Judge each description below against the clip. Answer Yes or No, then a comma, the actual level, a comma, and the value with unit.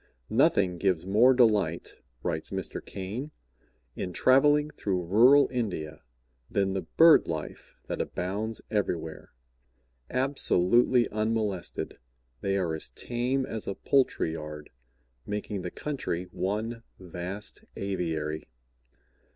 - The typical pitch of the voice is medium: No, low, 100 Hz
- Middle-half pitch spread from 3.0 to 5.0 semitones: No, wide, 5.4 semitones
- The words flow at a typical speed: No, slow, 110 wpm